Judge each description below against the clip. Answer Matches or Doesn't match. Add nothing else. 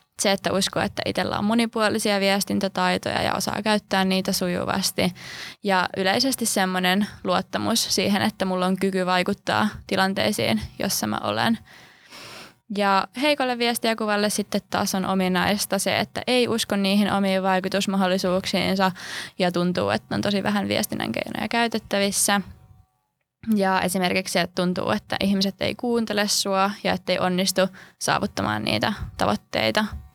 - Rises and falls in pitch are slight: Matches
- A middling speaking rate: Matches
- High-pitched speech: Matches